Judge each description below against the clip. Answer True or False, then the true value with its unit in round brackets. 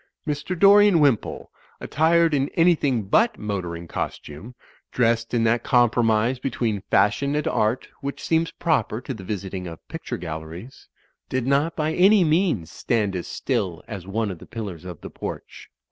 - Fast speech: False (160 wpm)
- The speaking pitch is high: False (120 Hz)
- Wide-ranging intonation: True (7.4 semitones)